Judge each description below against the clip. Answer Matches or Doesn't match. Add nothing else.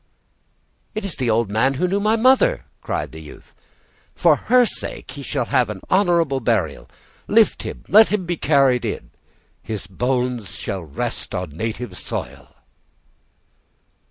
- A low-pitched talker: Matches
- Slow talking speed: Doesn't match